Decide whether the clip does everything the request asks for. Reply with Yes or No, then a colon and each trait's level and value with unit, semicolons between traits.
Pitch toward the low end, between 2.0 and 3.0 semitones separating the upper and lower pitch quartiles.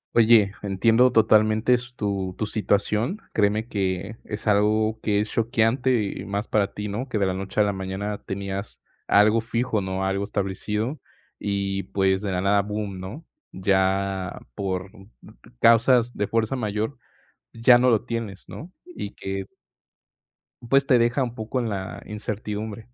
Yes: low, 105 Hz; average, 2.7 semitones